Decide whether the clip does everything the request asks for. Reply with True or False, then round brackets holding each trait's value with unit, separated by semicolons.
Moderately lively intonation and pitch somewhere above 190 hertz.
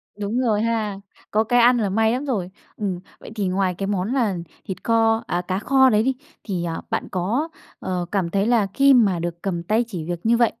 True (4.0 semitones; 210 Hz)